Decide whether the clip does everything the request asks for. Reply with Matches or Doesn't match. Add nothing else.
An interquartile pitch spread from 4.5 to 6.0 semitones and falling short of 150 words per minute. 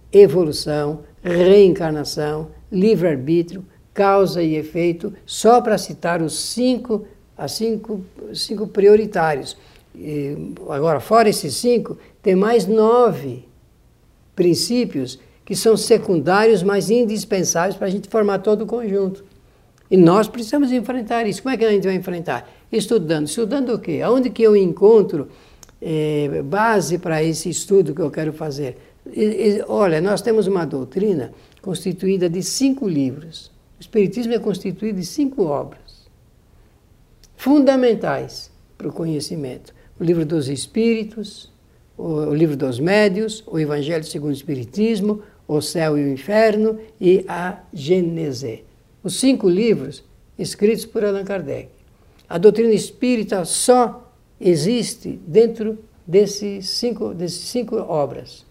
Matches